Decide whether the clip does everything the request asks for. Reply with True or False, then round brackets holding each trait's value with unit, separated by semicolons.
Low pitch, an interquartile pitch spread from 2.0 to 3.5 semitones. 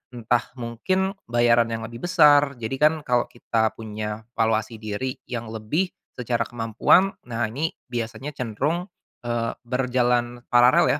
True (120 Hz; 2.6 semitones)